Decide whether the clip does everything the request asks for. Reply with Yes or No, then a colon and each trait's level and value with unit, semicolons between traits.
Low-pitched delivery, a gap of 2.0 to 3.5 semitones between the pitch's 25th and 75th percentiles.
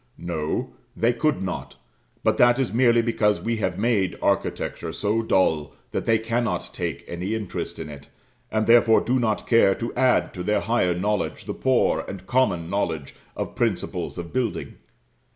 No: low, 105 Hz; average, 4.7 semitones